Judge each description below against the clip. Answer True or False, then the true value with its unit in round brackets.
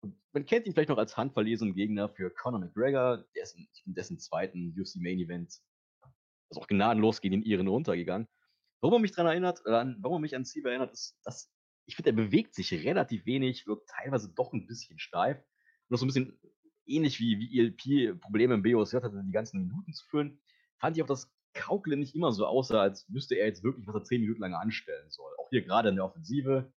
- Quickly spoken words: True (225 wpm)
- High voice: False (125 Hz)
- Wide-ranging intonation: True (6.4 semitones)